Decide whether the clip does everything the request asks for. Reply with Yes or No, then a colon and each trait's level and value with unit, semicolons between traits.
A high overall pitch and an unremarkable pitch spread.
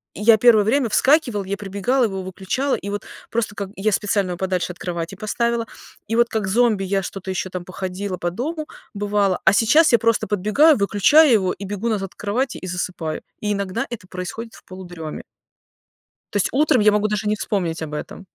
Yes: high, 205 Hz; average, 3.5 semitones